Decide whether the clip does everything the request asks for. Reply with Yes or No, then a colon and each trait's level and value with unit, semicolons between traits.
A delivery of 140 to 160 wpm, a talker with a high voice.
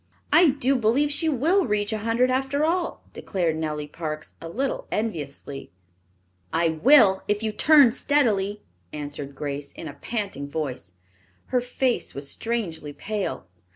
Yes: average, 145 wpm; high, 210 Hz